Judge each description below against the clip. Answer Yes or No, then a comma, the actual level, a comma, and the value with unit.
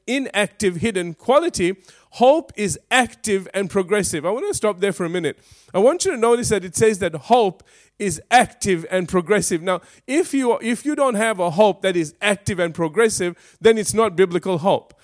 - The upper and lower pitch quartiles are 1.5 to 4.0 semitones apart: No, average, 4.4 semitones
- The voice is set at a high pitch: Yes, high, 205 Hz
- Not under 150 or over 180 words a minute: No, average, 195 wpm